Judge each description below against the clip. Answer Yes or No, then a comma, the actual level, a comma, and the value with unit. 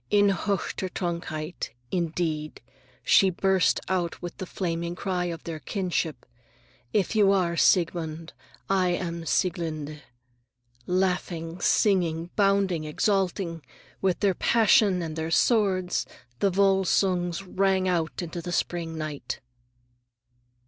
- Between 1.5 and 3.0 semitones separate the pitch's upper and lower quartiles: Yes, narrow, 2.6 semitones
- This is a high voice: No, medium, 175 Hz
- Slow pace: Yes, slow, 105 wpm